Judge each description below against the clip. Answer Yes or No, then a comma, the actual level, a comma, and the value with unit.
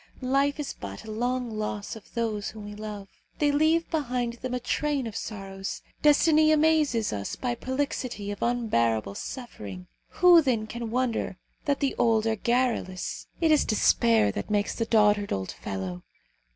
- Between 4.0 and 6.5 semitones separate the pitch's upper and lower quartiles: Yes, average, 4.7 semitones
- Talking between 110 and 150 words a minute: No, average, 165 wpm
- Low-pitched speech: No, high, 230 Hz